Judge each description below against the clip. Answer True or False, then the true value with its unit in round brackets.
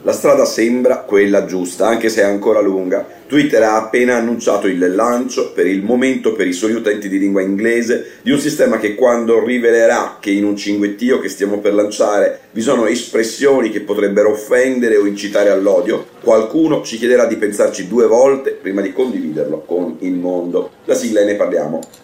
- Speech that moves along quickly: True (180 wpm)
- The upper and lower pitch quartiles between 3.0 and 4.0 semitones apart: True (3.6 semitones)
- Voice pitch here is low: True (105 Hz)